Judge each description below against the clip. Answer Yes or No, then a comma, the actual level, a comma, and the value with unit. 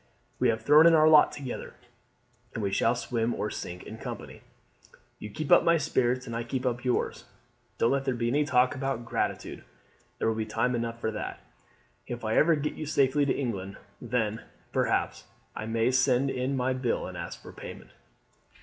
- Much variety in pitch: No, average, 3.2 semitones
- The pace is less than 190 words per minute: No, average, 195 wpm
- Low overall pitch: Yes, low, 125 Hz